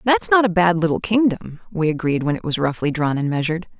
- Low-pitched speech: No, medium, 175 Hz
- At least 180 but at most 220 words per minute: No, fast, 235 wpm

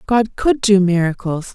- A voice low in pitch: No, high, 200 Hz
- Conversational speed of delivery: Yes, average, 155 wpm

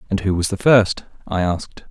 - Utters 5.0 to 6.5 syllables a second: Yes, 5.4 syllables/s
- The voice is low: Yes, low, 100 Hz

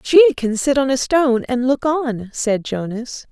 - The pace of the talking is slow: No, average, 200 wpm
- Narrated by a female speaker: Yes, female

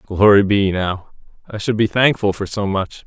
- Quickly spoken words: No, average, 195 wpm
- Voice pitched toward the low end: Yes, low, 100 Hz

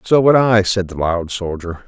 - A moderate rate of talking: No, fast, 225 wpm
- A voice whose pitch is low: Yes, low, 100 Hz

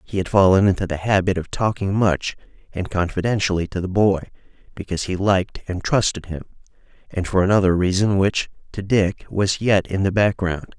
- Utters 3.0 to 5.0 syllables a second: No, 5.5 syllables/s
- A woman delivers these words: No, male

